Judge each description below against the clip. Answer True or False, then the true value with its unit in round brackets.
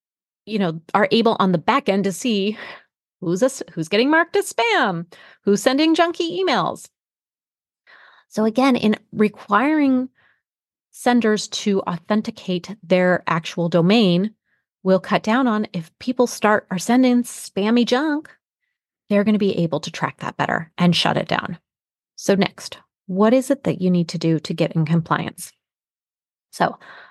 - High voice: True (210 Hz)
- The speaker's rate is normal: True (155 wpm)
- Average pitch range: False (5.7 semitones)